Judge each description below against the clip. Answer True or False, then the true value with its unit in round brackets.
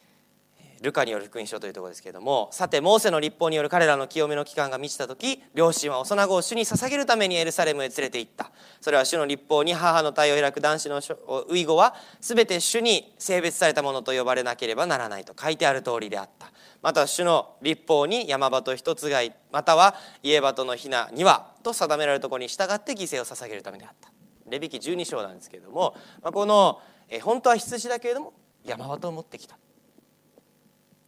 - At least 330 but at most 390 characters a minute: False (400 characters per minute)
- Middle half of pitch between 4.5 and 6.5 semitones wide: True (6.0 semitones)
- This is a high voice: False (155 Hz)